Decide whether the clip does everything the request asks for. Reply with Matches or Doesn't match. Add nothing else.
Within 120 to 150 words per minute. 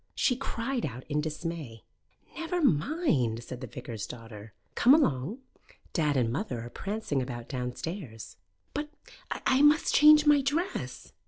Matches